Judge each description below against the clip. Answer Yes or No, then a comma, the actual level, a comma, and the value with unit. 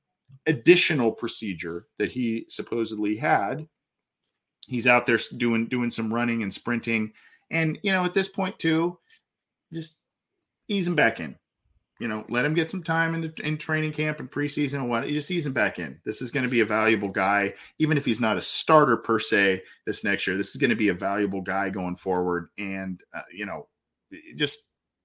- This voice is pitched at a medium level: No, low, 120 Hz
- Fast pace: No, average, 195 wpm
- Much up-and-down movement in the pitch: Yes, wide, 7.1 semitones